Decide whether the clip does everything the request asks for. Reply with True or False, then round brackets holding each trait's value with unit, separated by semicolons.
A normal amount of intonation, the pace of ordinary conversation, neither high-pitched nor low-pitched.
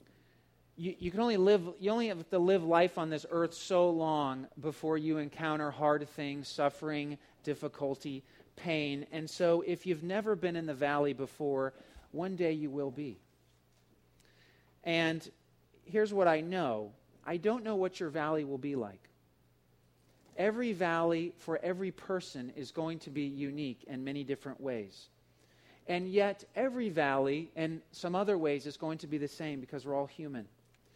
True (4.1 semitones; 165 wpm; 155 Hz)